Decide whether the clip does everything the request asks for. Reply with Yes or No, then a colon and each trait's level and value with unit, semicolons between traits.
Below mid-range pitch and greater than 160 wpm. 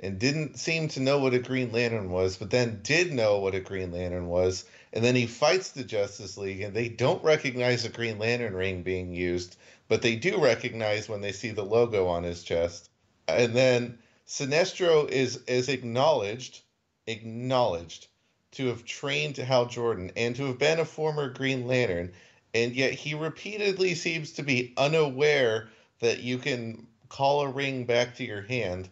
Yes: low, 120 Hz; average, 180 wpm